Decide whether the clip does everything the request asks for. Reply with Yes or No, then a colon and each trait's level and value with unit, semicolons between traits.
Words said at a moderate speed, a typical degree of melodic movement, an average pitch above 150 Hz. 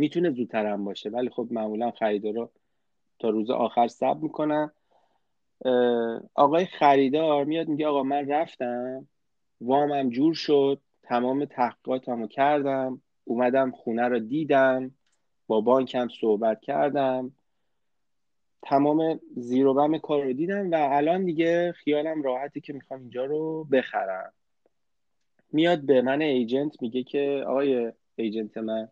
No: average, 130 wpm; average, 3.5 semitones; low, 135 Hz